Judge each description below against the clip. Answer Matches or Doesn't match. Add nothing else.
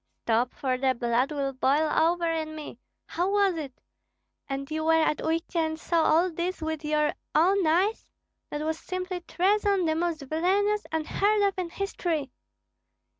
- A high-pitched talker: Matches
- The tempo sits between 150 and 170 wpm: Matches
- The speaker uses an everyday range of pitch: Matches